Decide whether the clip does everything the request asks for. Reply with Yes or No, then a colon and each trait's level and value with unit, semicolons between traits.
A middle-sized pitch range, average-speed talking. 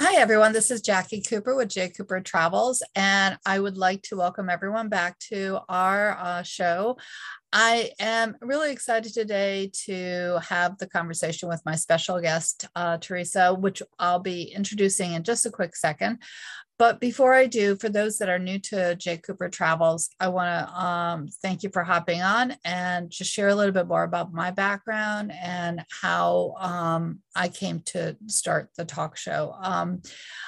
Yes: average, 3.4 semitones; average, 175 wpm